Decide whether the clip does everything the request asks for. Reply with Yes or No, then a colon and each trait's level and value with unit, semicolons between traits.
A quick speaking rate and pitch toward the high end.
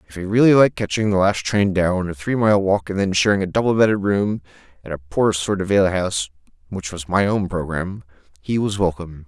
No: fast, 220 wpm; very low, 95 Hz